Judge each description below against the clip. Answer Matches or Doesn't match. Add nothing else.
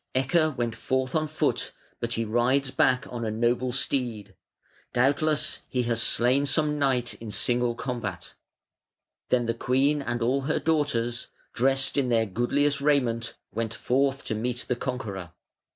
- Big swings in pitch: Doesn't match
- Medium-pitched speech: Doesn't match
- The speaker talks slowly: Doesn't match